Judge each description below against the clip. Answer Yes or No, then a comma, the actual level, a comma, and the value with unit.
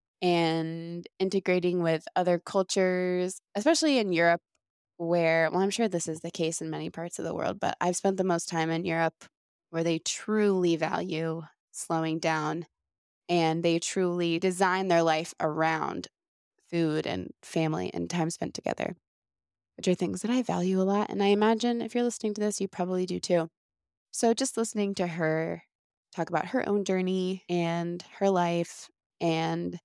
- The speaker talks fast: No, average, 170 wpm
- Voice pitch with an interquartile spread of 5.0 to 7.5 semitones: No, average, 2.9 semitones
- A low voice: No, medium, 175 Hz